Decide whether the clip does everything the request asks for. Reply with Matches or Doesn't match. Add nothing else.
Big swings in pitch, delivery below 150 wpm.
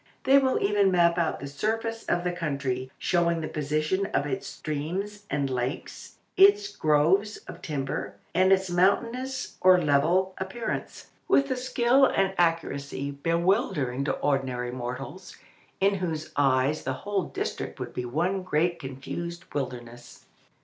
Matches